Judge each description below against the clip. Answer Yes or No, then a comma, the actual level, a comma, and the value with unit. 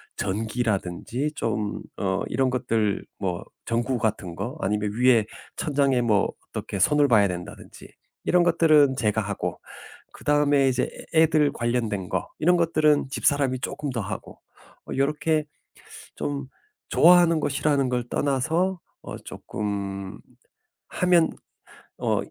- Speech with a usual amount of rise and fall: No, wide, 6.0 semitones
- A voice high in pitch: No, low, 125 Hz